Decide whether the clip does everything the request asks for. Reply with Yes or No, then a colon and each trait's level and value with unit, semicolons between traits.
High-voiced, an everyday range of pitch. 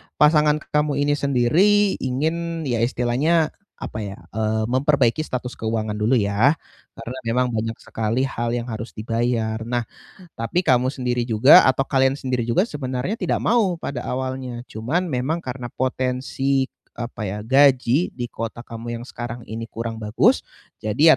No: low, 125 Hz; average, 3.5 semitones